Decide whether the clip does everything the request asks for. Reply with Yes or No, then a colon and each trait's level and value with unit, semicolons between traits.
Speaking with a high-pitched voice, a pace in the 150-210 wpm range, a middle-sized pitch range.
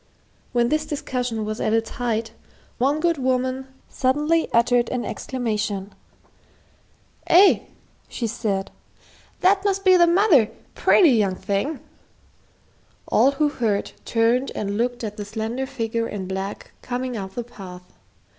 No: high, 240 Hz; slow, 135 wpm; average, 4.3 semitones